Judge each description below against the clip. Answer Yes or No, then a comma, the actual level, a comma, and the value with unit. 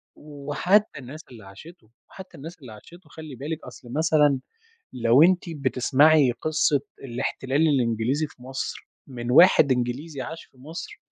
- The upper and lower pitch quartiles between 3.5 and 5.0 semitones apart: Yes, average, 4.1 semitones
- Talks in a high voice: No, medium, 140 Hz